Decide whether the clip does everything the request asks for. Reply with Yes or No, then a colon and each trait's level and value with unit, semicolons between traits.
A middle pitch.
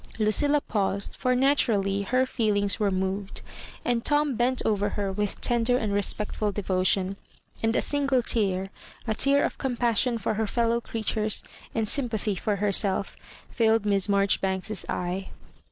No: high, 215 Hz